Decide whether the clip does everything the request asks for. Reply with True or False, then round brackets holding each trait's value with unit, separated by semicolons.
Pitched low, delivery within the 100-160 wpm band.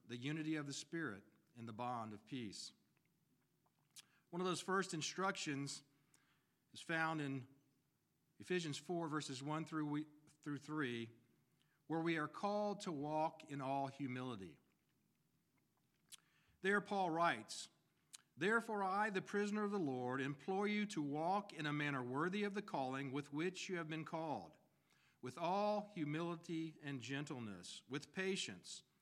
False (155 Hz; 140 wpm)